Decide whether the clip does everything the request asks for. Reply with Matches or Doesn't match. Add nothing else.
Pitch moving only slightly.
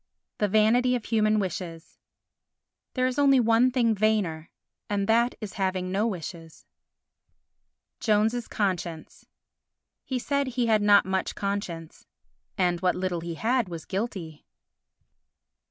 Doesn't match